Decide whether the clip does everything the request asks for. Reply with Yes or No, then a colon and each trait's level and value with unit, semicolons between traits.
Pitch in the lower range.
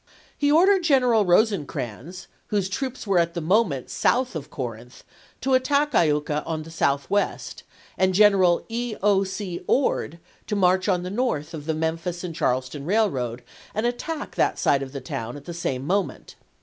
No: medium, 180 Hz